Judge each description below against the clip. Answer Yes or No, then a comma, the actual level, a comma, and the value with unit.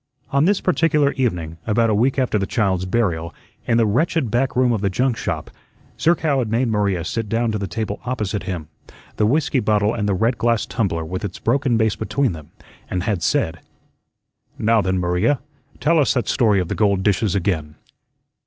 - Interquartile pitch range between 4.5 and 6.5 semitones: Yes, average, 4.8 semitones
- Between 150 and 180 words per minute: No, average, 195 wpm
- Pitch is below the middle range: Yes, low, 110 Hz